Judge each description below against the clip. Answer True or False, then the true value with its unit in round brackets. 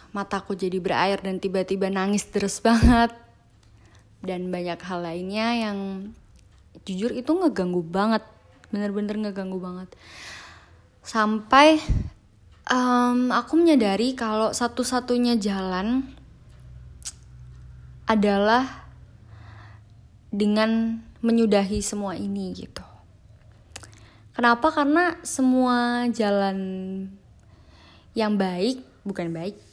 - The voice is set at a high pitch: True (200 Hz)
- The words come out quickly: False (85 wpm)